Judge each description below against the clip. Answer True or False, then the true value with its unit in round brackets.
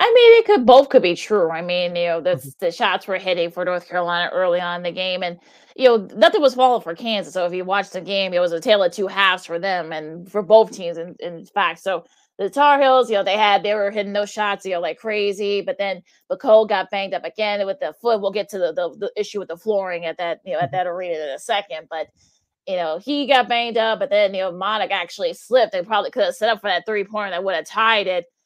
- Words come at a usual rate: False (280 wpm)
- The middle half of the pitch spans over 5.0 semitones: False (3.8 semitones)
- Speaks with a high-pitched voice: True (195 Hz)